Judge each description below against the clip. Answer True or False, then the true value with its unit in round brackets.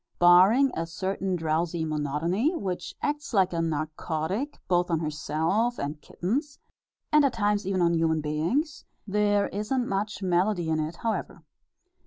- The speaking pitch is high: False (180 Hz)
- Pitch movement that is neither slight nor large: True (4.9 semitones)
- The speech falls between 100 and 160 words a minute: True (145 wpm)